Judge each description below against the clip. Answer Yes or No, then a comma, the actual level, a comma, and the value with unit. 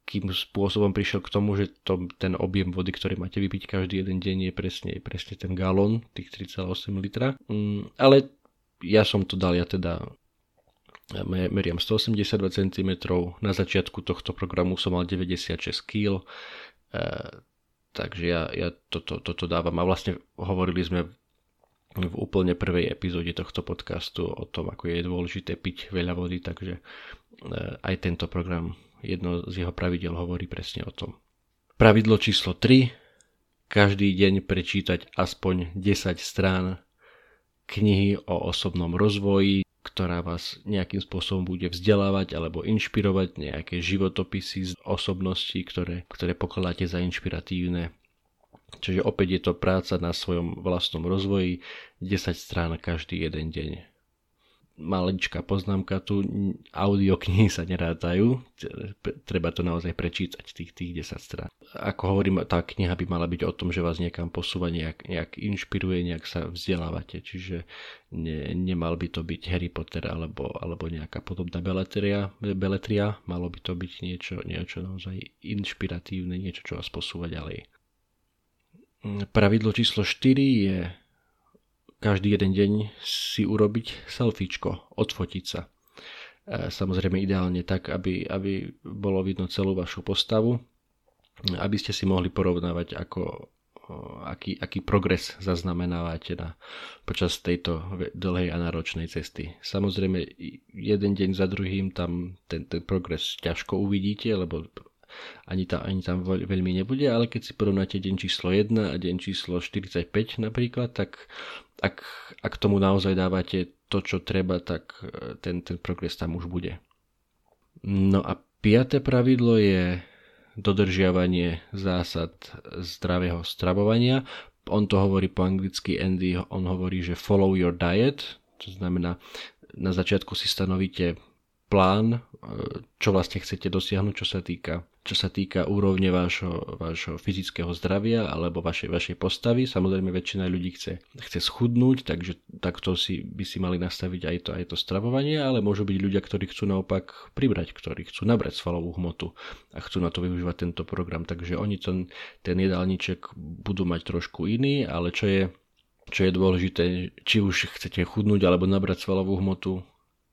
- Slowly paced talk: No, average, 140 wpm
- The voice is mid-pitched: No, very low, 95 Hz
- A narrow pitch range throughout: Yes, narrow, 2.1 semitones